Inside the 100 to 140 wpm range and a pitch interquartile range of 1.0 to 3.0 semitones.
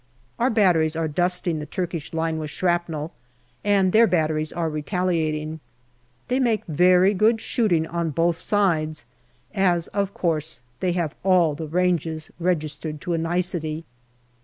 Yes: slow, 135 wpm; narrow, 2.6 semitones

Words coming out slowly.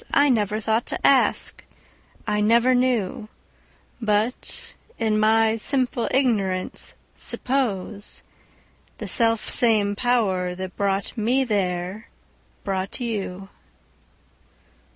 Yes: slow, 90 wpm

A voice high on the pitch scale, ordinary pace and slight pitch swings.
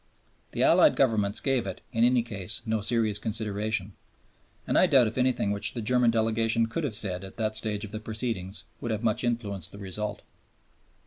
No: low, 110 Hz; average, 190 wpm; narrow, 2.2 semitones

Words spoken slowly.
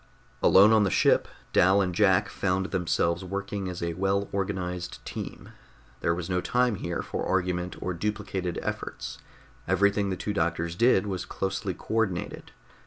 No: average, 160 wpm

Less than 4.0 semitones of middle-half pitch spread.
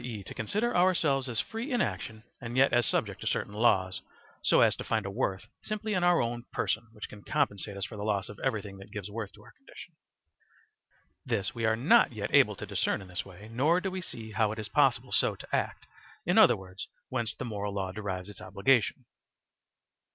No: average, 4.6 semitones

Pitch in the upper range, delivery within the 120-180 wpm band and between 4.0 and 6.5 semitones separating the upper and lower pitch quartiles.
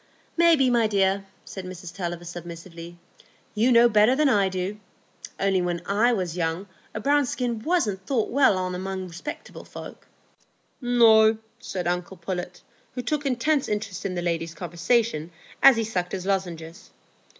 Yes: high, 195 Hz; average, 155 wpm; average, 4.9 semitones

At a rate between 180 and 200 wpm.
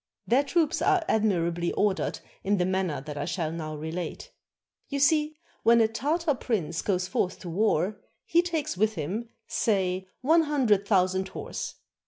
No: average, 160 wpm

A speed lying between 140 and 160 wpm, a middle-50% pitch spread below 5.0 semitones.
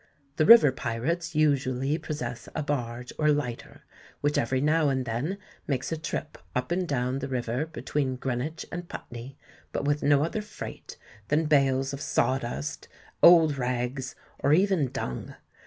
Yes: average, 155 wpm; average, 3.3 semitones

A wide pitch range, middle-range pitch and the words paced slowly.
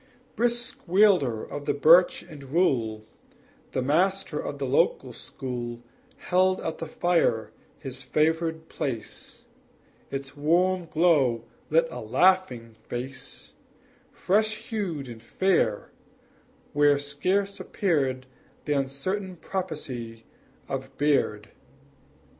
Yes: wide, 5.9 semitones; medium, 145 Hz; slow, 105 wpm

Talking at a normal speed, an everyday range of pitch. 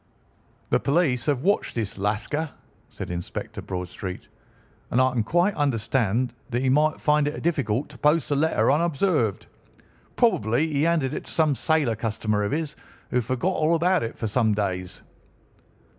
No: average, 160 wpm; wide, 6.0 semitones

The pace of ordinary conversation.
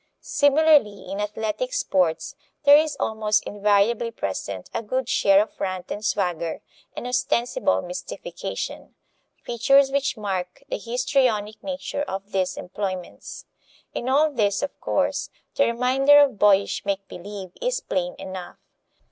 No: slow, 130 wpm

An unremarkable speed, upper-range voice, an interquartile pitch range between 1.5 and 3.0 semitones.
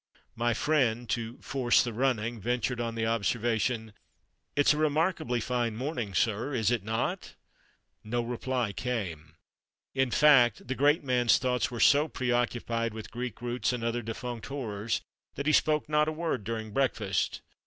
No: average, 155 wpm; low, 120 Hz; average, 2.7 semitones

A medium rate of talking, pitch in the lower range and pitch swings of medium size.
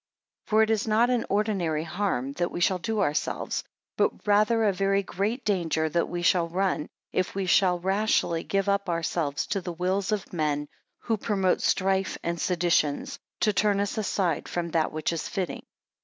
No: average, 185 wpm; high, 190 Hz; average, 3.3 semitones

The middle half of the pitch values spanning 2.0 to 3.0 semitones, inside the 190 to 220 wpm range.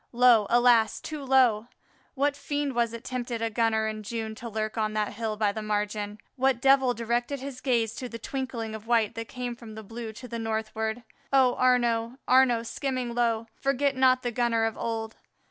Yes: narrow, 2.5 semitones; average, 195 wpm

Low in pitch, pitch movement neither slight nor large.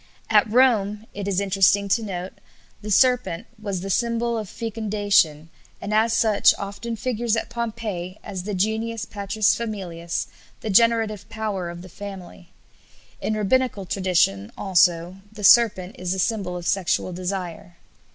No: high, 200 Hz; average, 3.3 semitones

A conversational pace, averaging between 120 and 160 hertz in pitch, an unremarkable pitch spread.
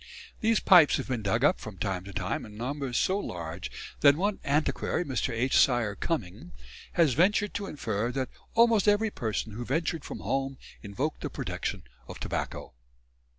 No: average, 170 wpm; low, 135 Hz; wide, 8.0 semitones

